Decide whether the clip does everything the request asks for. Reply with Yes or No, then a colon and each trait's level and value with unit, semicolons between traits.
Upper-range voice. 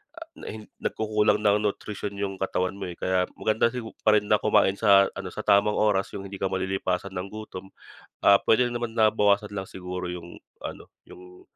No: low, 100 Hz